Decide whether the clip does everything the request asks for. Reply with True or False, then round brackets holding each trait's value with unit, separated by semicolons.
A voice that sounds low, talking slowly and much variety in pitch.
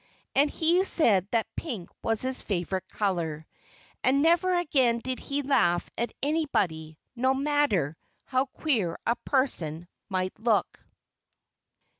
False (240 Hz; 125 wpm; 7.5 semitones)